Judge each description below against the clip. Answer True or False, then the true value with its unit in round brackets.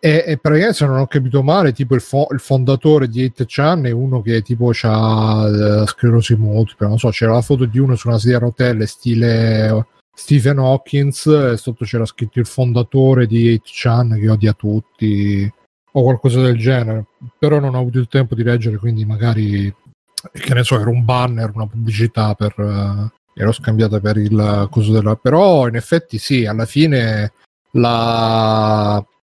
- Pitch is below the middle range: True (120 Hz)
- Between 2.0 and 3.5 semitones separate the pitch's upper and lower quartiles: True (3.2 semitones)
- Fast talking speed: True (180 wpm)